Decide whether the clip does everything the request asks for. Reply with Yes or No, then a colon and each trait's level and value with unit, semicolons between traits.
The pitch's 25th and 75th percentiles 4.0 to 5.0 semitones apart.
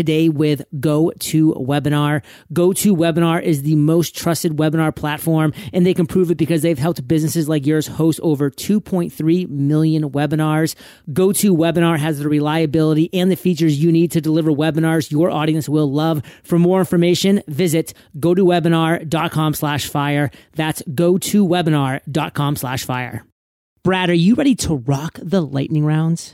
No: narrow, 2.4 semitones